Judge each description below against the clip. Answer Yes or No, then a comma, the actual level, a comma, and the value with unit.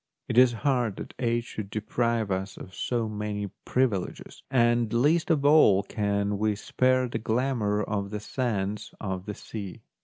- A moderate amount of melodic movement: Yes, average, 3.2 semitones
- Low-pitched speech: Yes, low, 110 Hz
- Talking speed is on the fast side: No, average, 160 wpm